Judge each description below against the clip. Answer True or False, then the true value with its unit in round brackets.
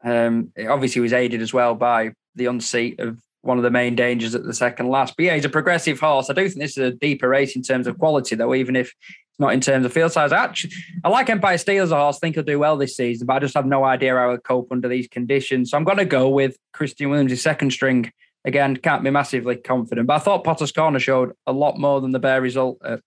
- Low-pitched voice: True (130 Hz)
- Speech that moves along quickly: True (270 wpm)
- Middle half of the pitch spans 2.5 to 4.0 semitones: True (2.9 semitones)